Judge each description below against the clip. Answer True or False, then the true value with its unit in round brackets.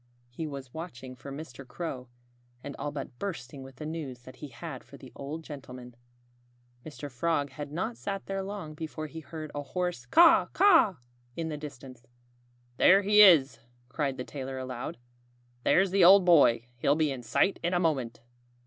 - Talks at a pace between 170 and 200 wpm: True (175 wpm)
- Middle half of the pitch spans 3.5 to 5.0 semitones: True (4.5 semitones)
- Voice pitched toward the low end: False (145 Hz)